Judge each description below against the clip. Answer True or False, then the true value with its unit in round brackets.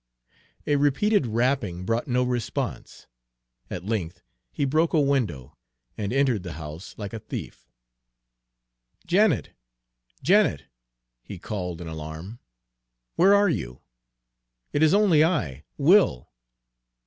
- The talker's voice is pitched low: True (120 Hz)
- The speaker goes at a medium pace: False (115 wpm)